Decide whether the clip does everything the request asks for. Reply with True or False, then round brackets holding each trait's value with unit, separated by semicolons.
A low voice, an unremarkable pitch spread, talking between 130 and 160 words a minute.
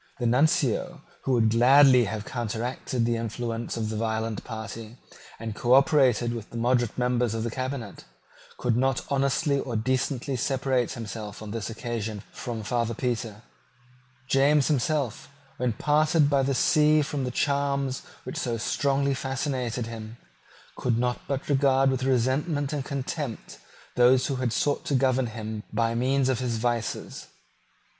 True (125 Hz; 3.0 semitones; 150 wpm)